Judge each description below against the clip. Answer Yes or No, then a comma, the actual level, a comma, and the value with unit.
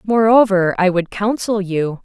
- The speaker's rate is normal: Yes, average, 145 wpm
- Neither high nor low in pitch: No, high, 195 Hz